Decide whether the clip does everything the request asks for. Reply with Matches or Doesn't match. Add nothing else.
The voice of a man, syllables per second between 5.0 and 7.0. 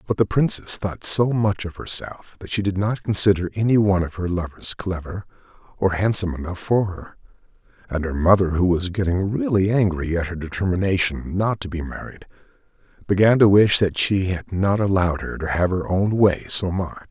Matches